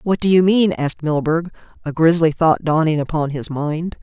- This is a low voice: No, medium, 160 Hz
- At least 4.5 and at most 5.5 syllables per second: Yes, 5.0 syllables/s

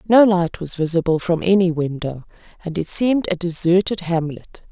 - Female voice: Yes, female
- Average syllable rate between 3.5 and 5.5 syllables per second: Yes, 5.2 syllables/s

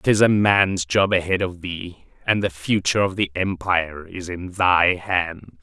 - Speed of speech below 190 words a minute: Yes, average, 180 wpm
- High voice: No, very low, 90 Hz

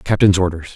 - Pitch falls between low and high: No, very low, 90 Hz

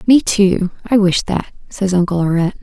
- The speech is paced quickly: No, average, 185 wpm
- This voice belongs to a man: No, female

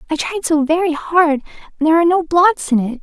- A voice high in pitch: Yes, very high, 320 Hz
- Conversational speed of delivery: No, fast, 240 wpm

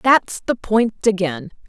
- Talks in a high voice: Yes, high, 200 Hz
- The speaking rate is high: No, average, 145 wpm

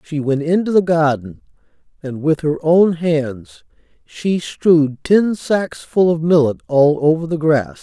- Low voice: No, medium, 160 Hz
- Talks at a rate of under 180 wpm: Yes, average, 160 wpm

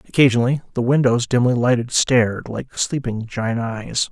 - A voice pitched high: No, low, 120 Hz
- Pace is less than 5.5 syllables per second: Yes, 5.0 syllables/s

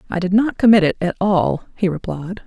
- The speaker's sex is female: Yes, female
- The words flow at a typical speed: No, fast, 220 wpm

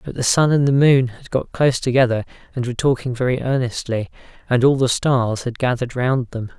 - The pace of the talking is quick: Yes, fast, 210 wpm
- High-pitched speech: No, low, 125 Hz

